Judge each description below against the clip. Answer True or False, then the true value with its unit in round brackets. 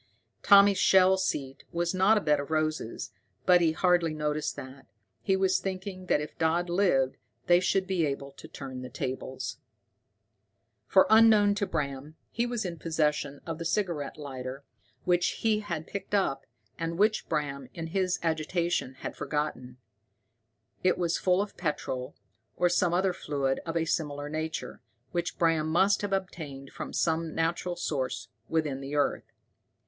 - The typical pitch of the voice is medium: True (165 Hz)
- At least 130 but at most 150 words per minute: False (160 wpm)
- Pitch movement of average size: True (4.2 semitones)